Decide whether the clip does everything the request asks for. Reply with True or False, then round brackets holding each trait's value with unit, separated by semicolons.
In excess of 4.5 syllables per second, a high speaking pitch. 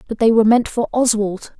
True (5.9 syllables/s; 225 Hz)